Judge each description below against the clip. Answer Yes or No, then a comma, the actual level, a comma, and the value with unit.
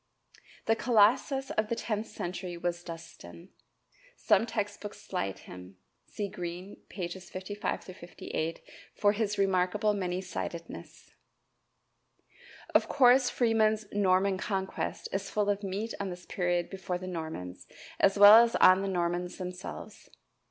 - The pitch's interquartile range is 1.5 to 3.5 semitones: Yes, average, 2.8 semitones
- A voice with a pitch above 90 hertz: Yes, high, 190 Hz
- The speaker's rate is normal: No, slow, 130 wpm